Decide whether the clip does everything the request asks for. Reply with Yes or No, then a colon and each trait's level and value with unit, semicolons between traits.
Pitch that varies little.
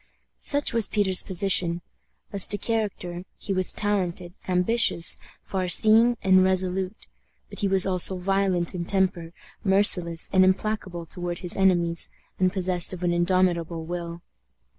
Yes: narrow, 2.0 semitones